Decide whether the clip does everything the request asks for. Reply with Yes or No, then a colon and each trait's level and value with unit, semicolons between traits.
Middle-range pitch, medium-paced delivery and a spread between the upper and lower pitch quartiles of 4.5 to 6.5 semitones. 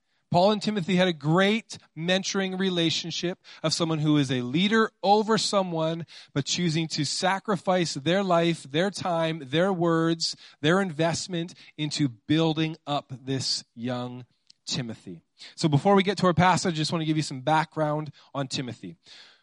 No: medium, 165 Hz; average, 160 wpm; average, 3.9 semitones